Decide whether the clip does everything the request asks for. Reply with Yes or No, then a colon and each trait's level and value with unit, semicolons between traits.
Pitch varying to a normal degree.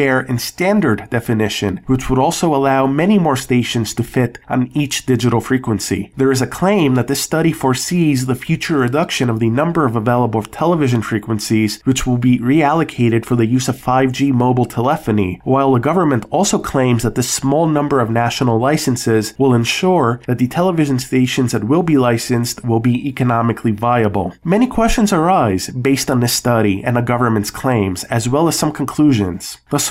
Yes: average, 3.6 semitones